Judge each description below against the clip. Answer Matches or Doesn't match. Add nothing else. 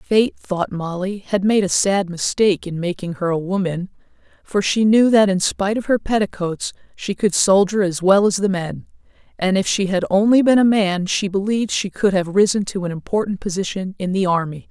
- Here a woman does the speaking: Matches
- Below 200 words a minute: Doesn't match